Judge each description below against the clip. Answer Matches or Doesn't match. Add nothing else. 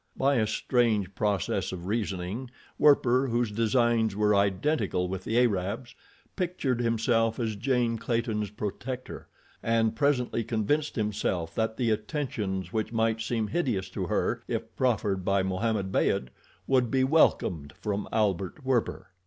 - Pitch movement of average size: Matches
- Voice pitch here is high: Doesn't match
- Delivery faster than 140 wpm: Doesn't match